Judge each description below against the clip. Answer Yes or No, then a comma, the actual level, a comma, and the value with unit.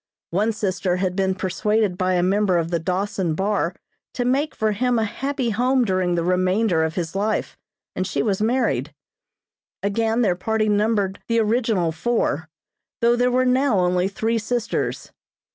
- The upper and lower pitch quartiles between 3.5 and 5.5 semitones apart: Yes, average, 4.0 semitones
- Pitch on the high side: Yes, high, 205 Hz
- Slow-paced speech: No, average, 165 wpm